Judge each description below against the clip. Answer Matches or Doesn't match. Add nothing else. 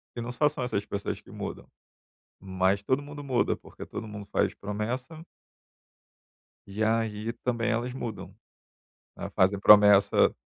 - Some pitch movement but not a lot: Matches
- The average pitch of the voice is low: Matches